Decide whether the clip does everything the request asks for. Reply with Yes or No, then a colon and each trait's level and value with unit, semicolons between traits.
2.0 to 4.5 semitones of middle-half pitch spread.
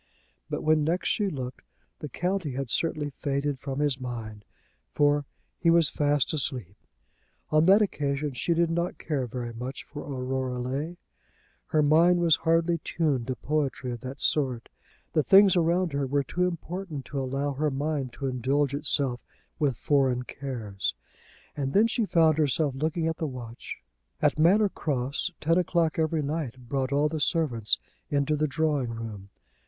Yes: average, 3.8 semitones